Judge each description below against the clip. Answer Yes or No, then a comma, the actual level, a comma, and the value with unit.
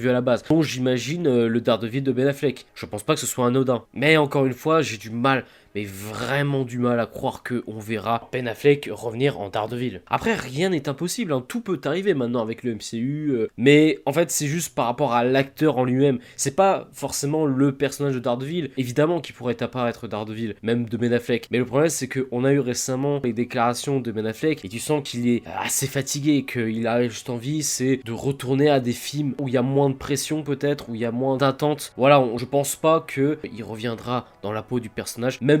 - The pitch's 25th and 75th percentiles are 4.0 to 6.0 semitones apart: No, average, 3.2 semitones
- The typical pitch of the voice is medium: No, low, 130 Hz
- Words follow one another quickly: Yes, fast, 235 wpm